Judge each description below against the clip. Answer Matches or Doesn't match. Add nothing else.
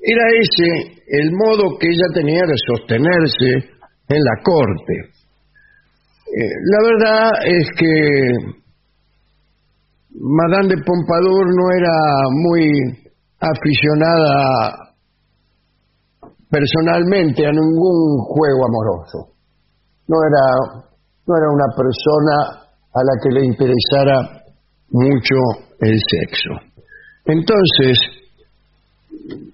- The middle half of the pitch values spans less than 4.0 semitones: Doesn't match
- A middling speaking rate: Doesn't match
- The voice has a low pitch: Doesn't match